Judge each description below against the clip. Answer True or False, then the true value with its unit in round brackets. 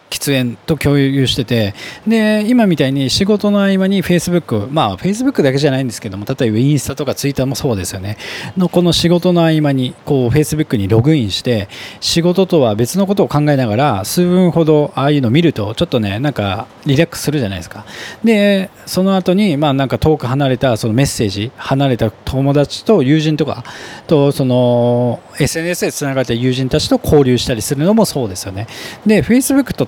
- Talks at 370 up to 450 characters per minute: True (410 characters per minute)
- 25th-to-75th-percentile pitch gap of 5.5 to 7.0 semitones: True (6.0 semitones)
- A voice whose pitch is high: False (140 Hz)